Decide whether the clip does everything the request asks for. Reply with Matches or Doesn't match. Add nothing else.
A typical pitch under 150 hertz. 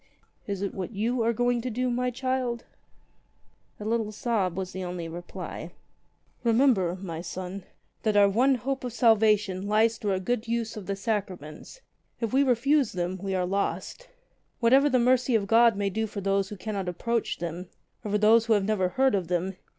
Doesn't match